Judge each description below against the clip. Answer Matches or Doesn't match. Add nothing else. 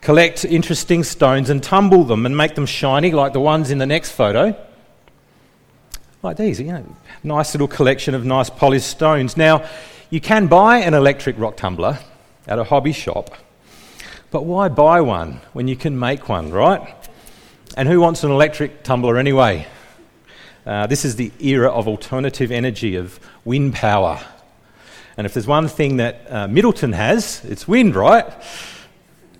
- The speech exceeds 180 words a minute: Doesn't match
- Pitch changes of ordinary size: Matches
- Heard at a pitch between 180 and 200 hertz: Doesn't match